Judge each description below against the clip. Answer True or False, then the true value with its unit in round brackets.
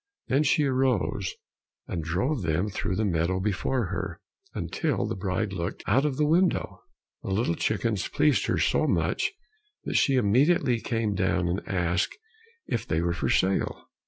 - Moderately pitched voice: False (105 Hz)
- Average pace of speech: True (160 wpm)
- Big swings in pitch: True (6.2 semitones)